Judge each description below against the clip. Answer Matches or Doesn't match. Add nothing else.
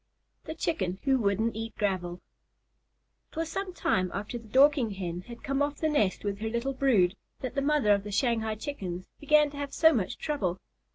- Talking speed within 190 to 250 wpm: Matches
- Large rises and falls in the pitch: Matches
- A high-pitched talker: Matches